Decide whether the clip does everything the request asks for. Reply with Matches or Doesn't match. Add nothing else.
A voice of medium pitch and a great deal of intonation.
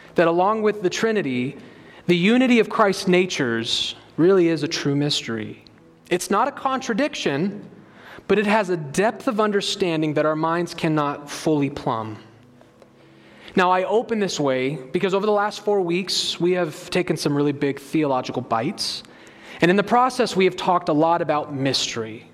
Matches